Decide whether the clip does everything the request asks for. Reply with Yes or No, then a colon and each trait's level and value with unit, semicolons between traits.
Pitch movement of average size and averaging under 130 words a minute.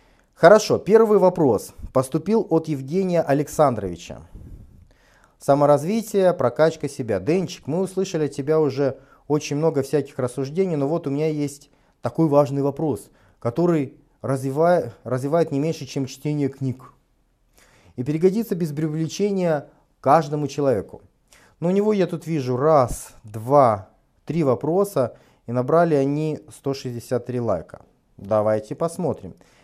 Yes: average, 3.5 semitones; average, 120 wpm